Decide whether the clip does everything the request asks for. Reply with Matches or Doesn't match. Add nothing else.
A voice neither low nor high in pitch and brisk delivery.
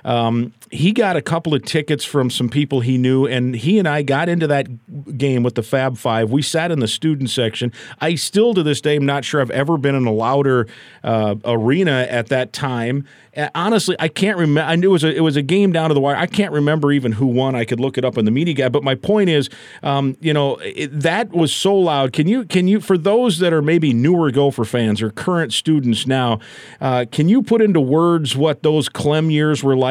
Matches